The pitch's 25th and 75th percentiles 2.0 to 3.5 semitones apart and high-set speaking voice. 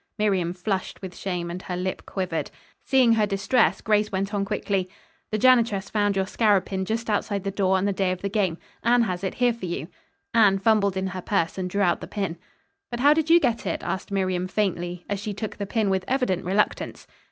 Yes: narrow, 2.5 semitones; high, 195 Hz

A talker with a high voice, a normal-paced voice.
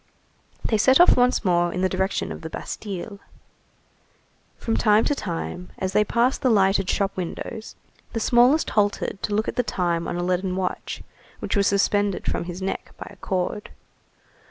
Yes: high, 200 Hz; average, 180 wpm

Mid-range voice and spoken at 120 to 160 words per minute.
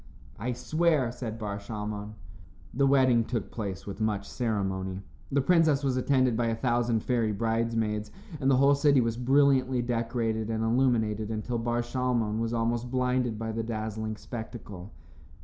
No: low, 115 Hz; average, 155 wpm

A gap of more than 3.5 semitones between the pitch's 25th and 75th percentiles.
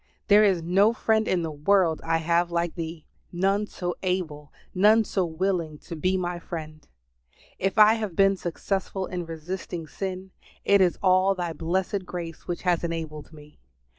No: average, 2.8 semitones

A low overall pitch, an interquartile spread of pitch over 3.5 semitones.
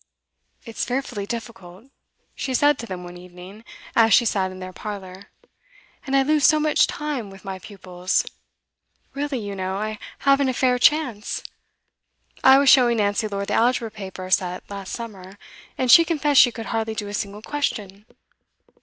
No: high, 215 Hz; average, 5.0 semitones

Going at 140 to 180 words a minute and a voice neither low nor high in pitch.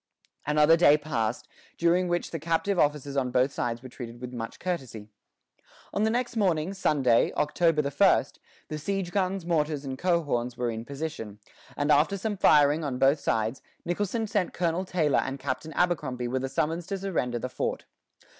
Yes: average, 175 wpm; medium, 150 Hz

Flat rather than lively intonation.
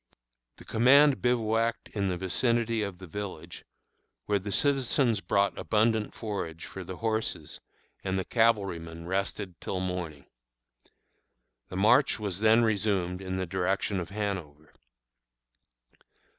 No: average, 3.5 semitones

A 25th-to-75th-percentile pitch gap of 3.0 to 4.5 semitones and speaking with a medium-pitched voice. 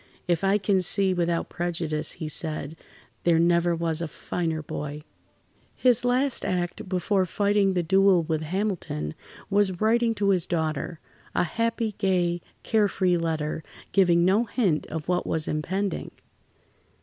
Yes: average, 3.5 semitones; medium, 175 Hz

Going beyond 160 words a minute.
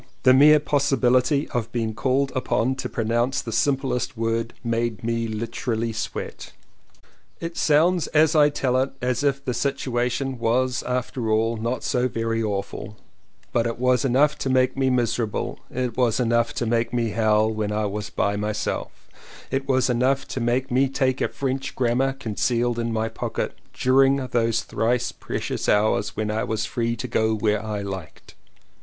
Yes: average, 170 wpm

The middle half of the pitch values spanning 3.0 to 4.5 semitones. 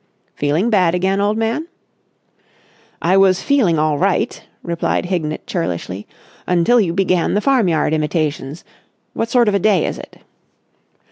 No: average, 4.9 semitones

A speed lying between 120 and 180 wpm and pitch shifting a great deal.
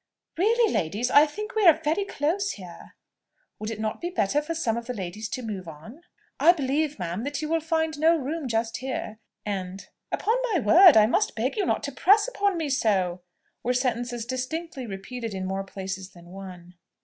No: average, 195 wpm; wide, 8.3 semitones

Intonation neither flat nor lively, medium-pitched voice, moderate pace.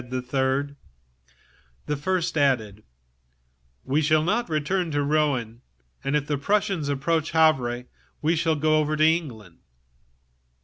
No: average, 3.2 semitones; medium, 150 Hz; slow, 120 wpm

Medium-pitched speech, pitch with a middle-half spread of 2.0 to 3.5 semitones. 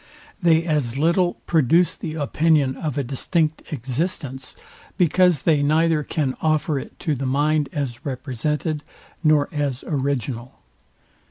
Yes: medium, 150 Hz; average, 3.0 semitones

